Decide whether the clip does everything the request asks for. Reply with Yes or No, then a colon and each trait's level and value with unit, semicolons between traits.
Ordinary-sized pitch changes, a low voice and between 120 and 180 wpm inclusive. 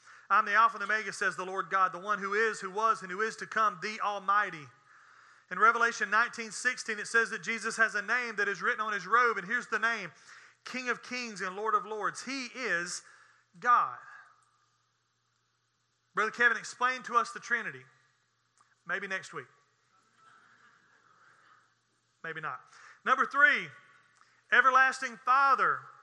No: average, 3.3 semitones; high, 230 Hz; average, 160 wpm